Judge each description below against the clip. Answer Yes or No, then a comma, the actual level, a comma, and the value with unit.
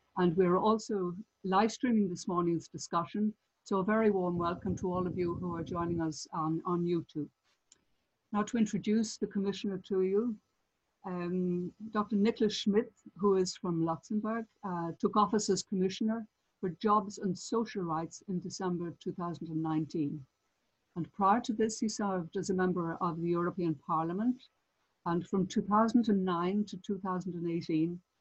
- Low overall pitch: No, medium, 185 Hz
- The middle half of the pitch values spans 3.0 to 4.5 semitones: Yes, average, 3.5 semitones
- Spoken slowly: No, average, 150 wpm